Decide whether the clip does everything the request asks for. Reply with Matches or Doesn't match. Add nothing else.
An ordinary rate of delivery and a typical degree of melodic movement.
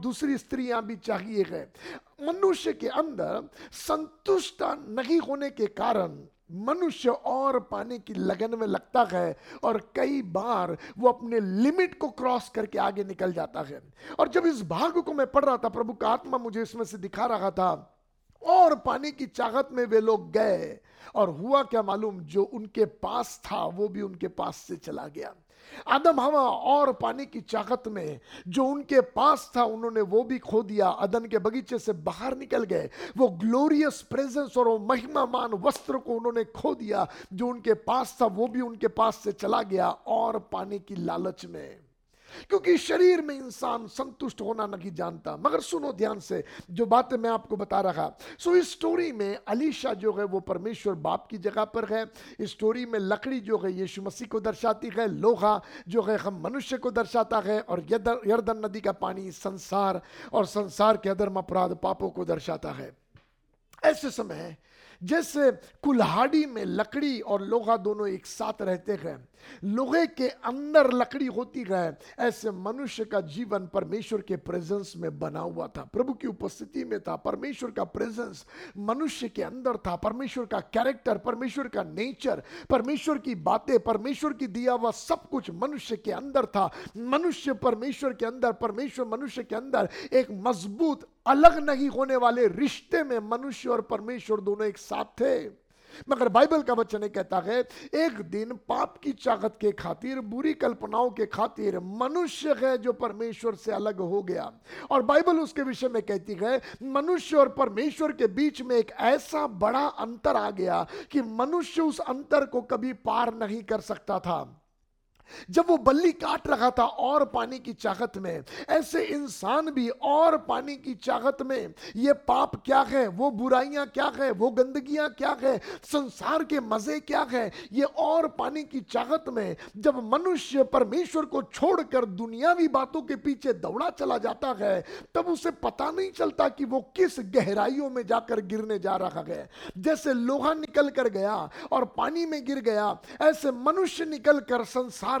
Matches